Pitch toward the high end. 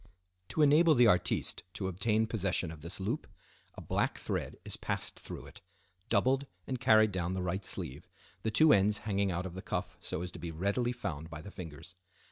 No: low, 100 Hz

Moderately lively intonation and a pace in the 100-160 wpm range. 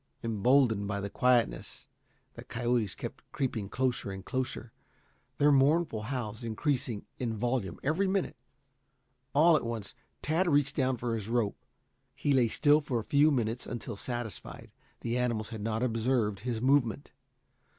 Yes: average, 3.6 semitones; average, 150 wpm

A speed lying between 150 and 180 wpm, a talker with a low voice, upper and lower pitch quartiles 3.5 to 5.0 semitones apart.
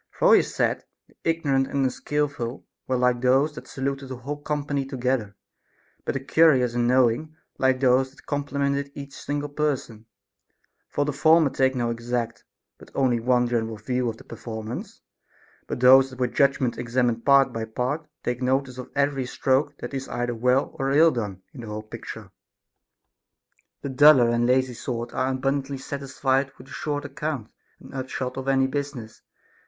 No: average, 170 wpm; low, 130 Hz; narrow, 2.4 semitones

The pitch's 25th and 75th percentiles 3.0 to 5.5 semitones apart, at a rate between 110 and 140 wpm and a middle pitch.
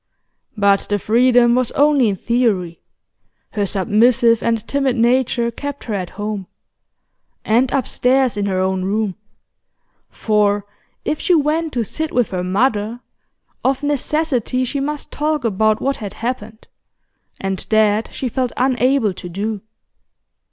No: average, 4.2 semitones; slow, 135 wpm; high, 235 Hz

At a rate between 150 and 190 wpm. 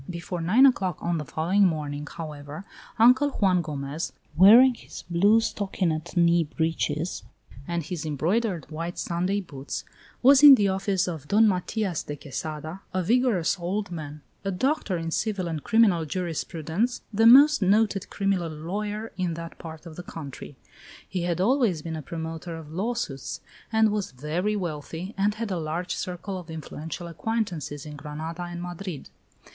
Yes: average, 160 wpm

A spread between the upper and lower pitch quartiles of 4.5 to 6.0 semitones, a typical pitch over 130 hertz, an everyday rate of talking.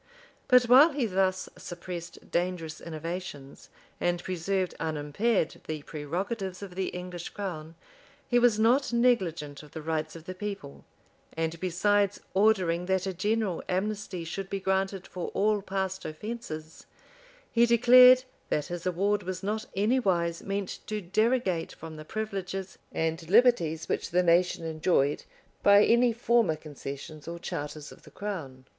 No: average, 4.1 semitones; medium, 185 Hz; average, 145 wpm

